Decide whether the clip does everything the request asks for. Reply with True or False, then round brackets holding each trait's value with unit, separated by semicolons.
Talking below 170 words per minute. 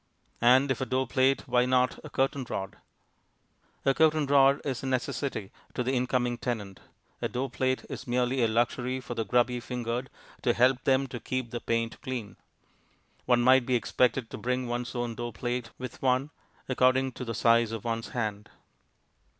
False (180 wpm)